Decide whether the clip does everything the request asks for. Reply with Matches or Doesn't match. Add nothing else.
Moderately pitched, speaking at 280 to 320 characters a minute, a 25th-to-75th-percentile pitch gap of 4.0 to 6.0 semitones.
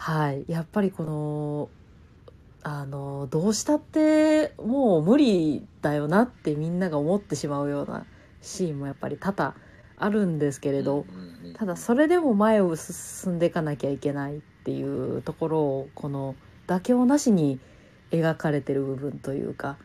Matches